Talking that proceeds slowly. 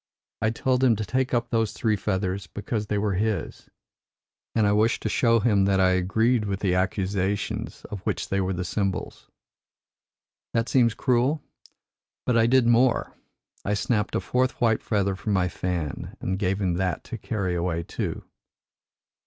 No: average, 170 wpm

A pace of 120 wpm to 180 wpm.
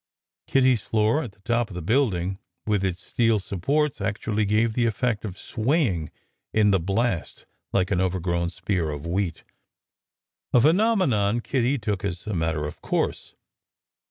Yes: average, 160 wpm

